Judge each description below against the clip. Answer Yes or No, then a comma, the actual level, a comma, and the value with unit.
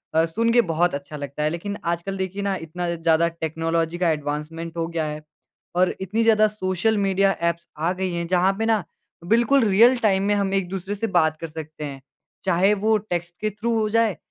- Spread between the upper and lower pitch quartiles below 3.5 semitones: No, average, 3.8 semitones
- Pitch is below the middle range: No, medium, 175 Hz